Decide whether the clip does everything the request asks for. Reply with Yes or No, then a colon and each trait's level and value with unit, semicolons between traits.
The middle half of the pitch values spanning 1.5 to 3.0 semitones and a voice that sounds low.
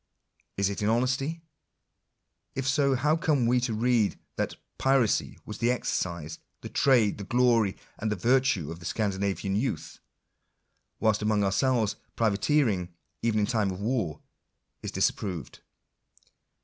No: average, 4.3 semitones; low, 110 Hz